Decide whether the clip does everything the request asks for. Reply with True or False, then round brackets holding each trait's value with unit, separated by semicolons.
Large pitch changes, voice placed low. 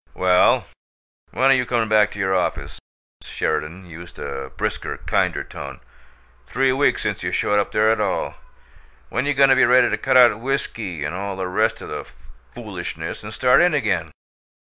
True (5.9 semitones; 105 Hz)